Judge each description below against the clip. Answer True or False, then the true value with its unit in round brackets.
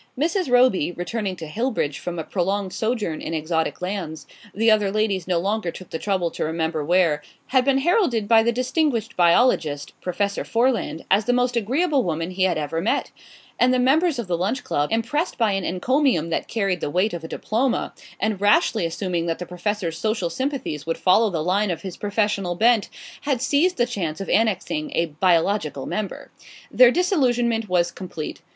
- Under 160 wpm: False (185 wpm)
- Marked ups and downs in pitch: True (5.9 semitones)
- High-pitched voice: True (205 Hz)